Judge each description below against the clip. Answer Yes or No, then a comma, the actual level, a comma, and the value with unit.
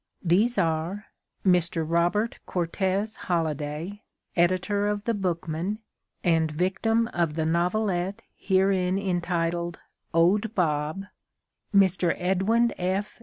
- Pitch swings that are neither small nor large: Yes, average, 3.1 semitones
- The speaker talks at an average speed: No, slow, 100 wpm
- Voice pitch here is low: No, medium, 180 Hz